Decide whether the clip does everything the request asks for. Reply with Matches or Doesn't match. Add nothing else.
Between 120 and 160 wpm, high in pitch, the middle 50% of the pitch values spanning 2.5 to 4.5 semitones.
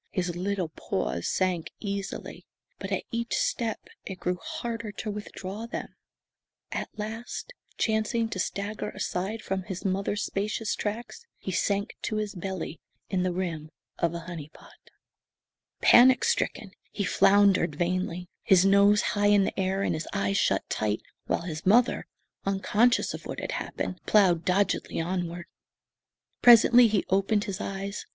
Matches